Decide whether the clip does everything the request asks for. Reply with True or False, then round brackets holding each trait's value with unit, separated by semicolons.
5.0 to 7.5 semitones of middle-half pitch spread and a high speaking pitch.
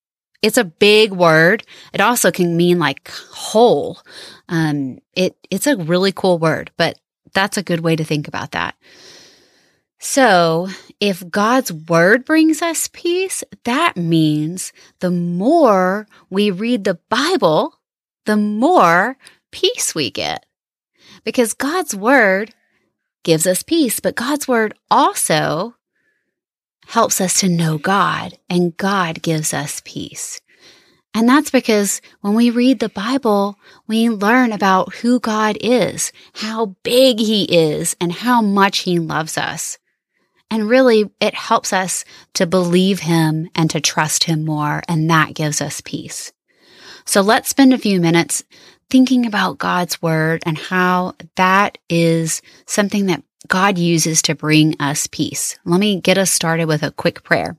True (5.5 semitones; 195 Hz)